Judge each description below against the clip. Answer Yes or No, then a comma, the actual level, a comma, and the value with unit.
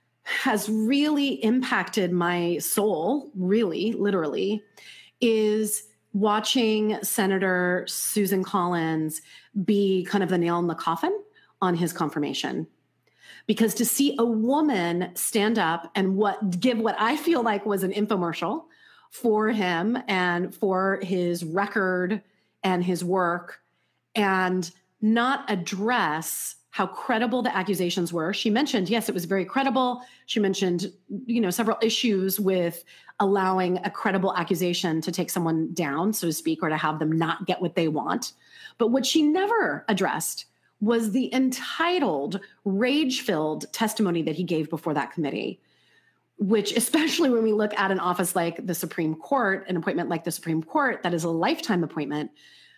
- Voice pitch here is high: Yes, high, 195 Hz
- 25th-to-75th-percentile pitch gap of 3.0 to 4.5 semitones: Yes, average, 4.2 semitones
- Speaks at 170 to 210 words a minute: No, average, 150 wpm